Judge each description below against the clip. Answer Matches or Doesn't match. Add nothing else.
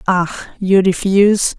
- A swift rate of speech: Doesn't match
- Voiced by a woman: Matches